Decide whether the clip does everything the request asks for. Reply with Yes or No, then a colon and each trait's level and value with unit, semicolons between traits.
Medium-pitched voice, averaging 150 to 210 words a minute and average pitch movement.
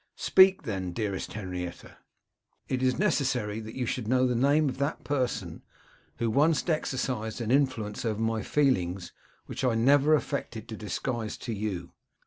No: low, 120 Hz; average, 155 wpm; average, 4.4 semitones